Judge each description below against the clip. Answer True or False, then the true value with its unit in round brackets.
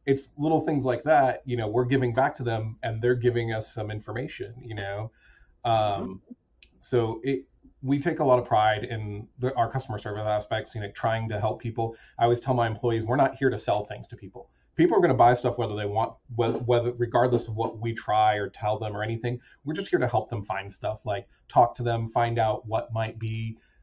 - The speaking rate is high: True (230 wpm)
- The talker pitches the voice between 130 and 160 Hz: False (115 Hz)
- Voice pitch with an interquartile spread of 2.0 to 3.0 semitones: True (2.4 semitones)